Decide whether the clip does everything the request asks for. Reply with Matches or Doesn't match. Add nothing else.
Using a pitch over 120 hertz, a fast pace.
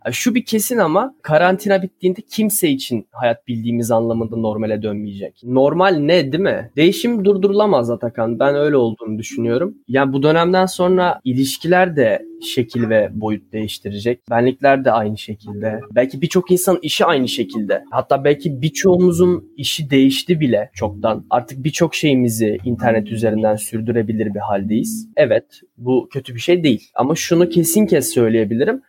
Matches